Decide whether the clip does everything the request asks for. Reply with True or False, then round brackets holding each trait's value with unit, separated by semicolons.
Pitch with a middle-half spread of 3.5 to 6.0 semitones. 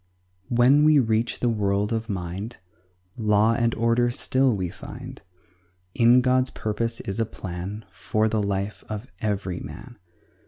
False (2.9 semitones)